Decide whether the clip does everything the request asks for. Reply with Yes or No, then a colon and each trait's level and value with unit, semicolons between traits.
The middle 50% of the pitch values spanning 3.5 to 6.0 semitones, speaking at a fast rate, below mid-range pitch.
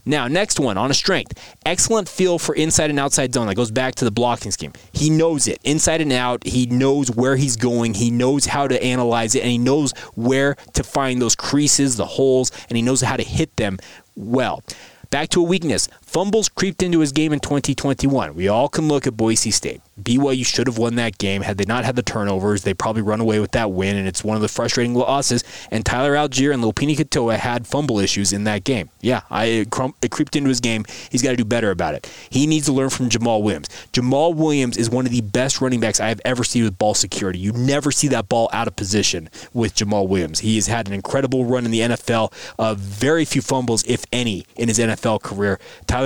Yes: average, 4.0 semitones; fast, 235 wpm; low, 125 Hz